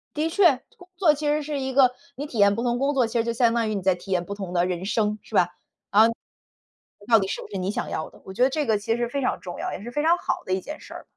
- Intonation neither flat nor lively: No, wide, 5.9 semitones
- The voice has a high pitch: Yes, high, 235 Hz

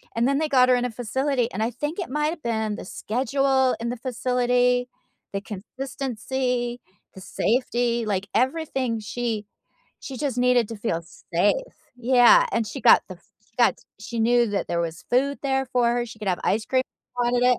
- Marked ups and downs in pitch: No, average, 2.7 semitones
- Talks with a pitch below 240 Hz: No, high, 245 Hz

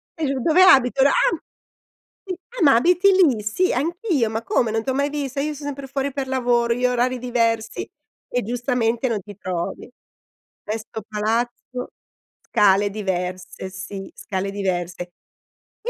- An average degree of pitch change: Yes, average, 4.9 semitones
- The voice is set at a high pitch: Yes, high, 240 Hz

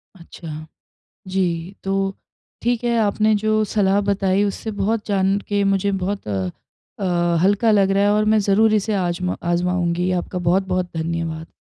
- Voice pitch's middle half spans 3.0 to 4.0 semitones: No, narrow, 2.6 semitones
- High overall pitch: Yes, high, 195 Hz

